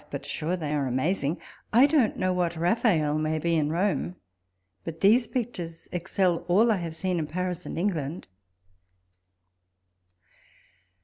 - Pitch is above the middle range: No, medium, 175 Hz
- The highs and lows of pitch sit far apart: No, average, 3.5 semitones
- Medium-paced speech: Yes, average, 145 wpm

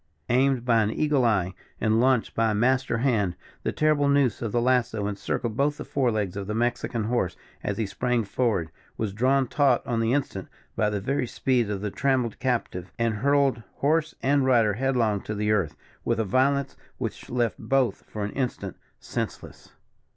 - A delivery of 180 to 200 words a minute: Yes, average, 185 wpm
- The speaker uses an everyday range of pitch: Yes, average, 3.8 semitones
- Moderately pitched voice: No, low, 120 Hz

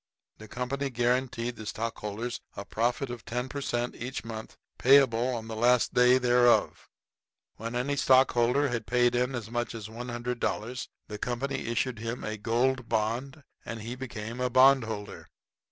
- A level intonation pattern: Yes, narrow, 1.9 semitones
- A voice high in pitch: No, low, 120 Hz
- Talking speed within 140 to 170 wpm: Yes, average, 155 wpm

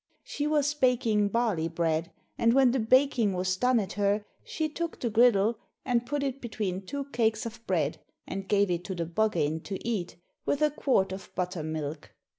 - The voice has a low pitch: No, high, 215 Hz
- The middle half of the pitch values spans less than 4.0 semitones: No, wide, 5.4 semitones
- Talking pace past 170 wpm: Yes, average, 185 wpm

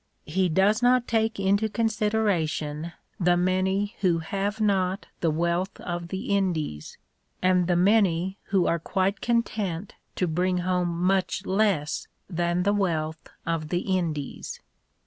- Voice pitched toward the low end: No, medium, 185 Hz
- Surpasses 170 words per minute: No, slow, 135 wpm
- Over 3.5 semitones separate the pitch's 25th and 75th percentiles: No, average, 2.9 semitones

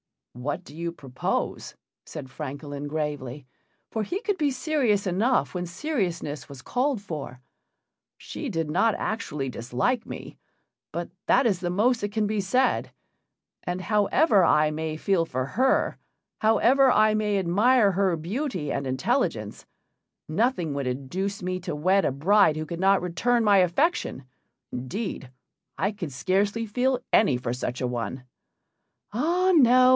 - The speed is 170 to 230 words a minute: No, average, 150 wpm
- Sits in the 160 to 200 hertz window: Yes, medium, 185 Hz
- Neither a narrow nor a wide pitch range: No, wide, 7.1 semitones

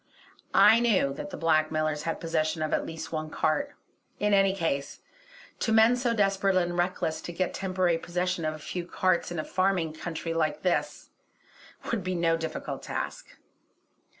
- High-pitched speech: No, medium, 175 Hz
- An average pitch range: Yes, average, 3.3 semitones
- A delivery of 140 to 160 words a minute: No, average, 170 wpm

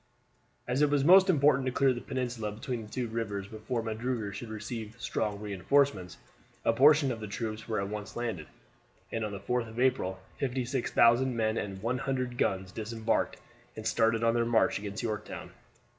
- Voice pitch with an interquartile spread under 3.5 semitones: Yes, average, 3.1 semitones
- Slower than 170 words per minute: No, average, 175 wpm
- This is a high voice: No, low, 115 Hz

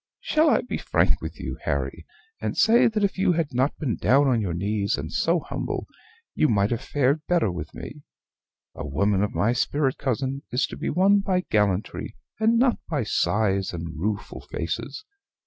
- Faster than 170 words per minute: Yes, average, 185 wpm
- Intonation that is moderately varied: No, wide, 8.8 semitones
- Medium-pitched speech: No, low, 130 Hz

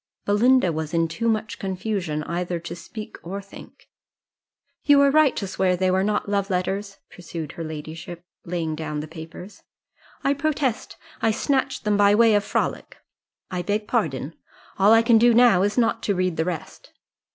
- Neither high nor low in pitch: No, high, 195 Hz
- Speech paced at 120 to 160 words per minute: No, average, 175 wpm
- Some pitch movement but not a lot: Yes, average, 4.7 semitones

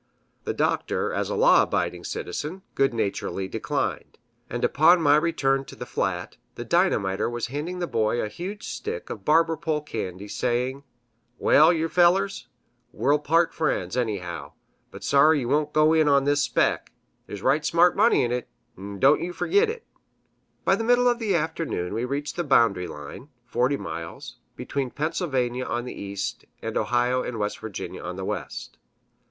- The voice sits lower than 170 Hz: Yes, medium, 140 Hz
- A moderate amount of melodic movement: No, wide, 5.7 semitones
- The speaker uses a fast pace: No, average, 170 wpm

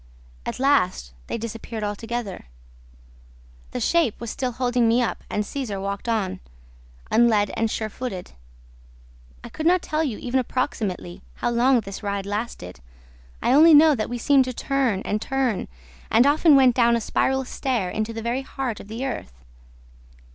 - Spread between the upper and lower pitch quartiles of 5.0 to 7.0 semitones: No, average, 4.1 semitones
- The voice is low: No, high, 235 Hz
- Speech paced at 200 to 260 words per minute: No, average, 165 wpm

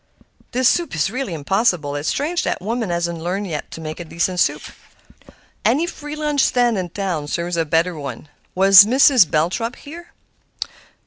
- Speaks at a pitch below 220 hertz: Yes, high, 190 Hz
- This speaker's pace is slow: No, average, 170 wpm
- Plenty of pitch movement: Yes, wide, 7.2 semitones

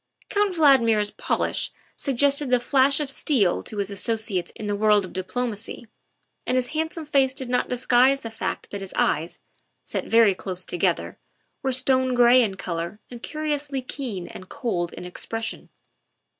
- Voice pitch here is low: No, high, 245 Hz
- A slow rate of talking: No, average, 170 wpm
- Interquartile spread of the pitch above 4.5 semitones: Yes, average, 5.0 semitones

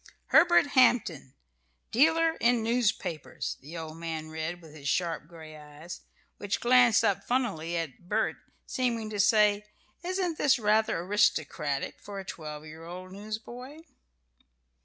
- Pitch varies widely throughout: Yes, wide, 7.0 semitones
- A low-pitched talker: No, high, 200 Hz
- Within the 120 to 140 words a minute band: Yes, slow, 135 wpm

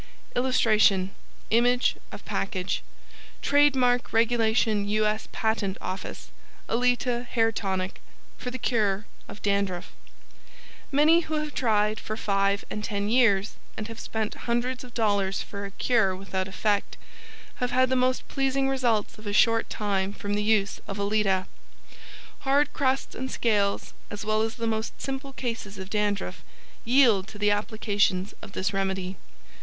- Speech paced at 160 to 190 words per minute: No, average, 150 wpm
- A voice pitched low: No, high, 215 Hz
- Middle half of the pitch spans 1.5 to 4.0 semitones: Yes, average, 3.5 semitones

